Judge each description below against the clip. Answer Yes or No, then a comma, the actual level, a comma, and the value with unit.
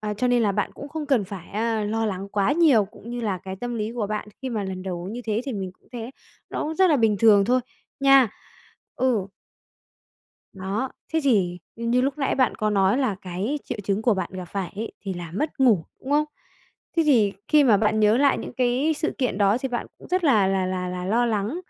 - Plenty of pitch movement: No, average, 4.7 semitones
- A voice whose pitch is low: No, high, 220 Hz